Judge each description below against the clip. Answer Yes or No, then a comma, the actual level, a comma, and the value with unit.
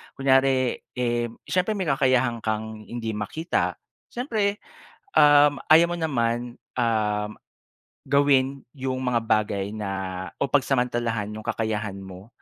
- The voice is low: Yes, low, 125 Hz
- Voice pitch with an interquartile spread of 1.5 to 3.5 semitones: No, average, 4.4 semitones